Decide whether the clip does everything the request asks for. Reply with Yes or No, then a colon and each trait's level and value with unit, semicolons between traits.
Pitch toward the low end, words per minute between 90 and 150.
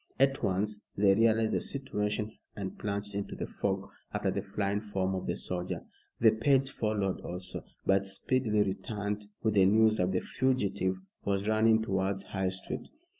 No: low, 105 Hz; average, 165 wpm